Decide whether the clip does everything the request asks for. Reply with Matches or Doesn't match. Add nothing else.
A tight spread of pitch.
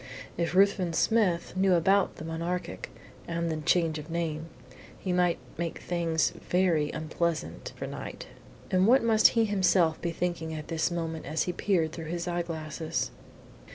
Matches